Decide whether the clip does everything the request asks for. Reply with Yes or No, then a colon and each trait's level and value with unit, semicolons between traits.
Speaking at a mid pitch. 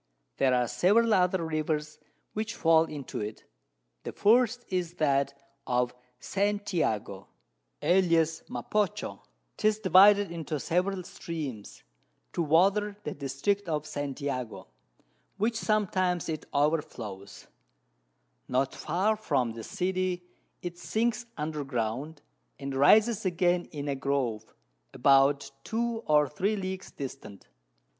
Yes: medium, 160 Hz